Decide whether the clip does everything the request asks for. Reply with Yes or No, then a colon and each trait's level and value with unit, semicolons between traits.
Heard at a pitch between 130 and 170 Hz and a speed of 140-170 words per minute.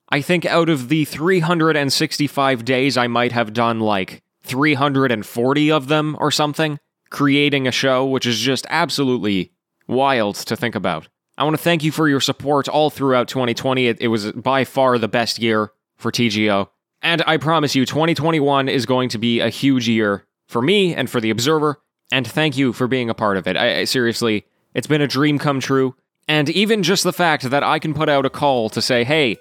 No: low, 135 Hz; fast, 205 wpm